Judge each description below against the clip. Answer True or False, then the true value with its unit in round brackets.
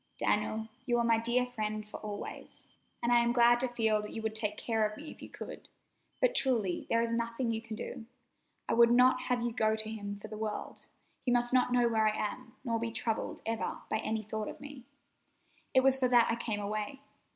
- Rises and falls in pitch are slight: True (2.0 semitones)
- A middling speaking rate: False (230 wpm)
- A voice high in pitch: True (230 Hz)